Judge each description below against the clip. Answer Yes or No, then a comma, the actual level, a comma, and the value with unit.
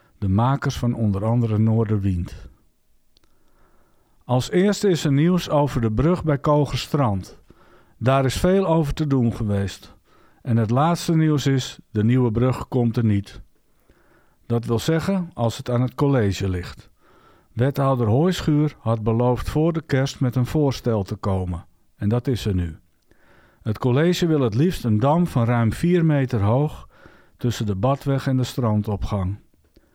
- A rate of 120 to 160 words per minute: Yes, average, 155 wpm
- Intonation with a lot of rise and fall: No, average, 5.0 semitones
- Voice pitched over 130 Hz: No, low, 125 Hz